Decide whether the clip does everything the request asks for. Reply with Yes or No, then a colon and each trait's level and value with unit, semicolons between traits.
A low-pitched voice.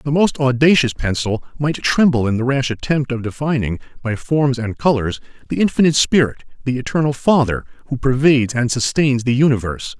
Yes: low, 130 Hz